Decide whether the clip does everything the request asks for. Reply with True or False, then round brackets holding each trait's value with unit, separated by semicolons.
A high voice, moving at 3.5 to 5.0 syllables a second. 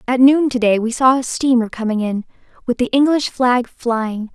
True (245 Hz; 4.8 syllables/s)